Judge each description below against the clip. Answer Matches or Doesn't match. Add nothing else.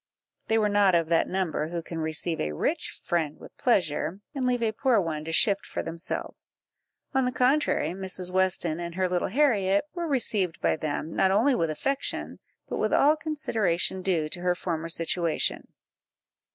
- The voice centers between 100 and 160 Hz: Doesn't match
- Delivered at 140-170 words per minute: Doesn't match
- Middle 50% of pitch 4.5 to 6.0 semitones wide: Matches